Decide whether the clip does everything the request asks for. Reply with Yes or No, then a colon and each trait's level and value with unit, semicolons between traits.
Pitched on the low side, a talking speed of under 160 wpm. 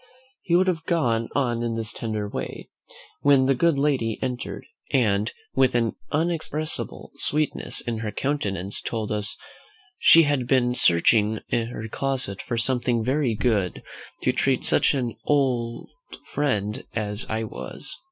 Yes: low, 120 Hz; average, 140 wpm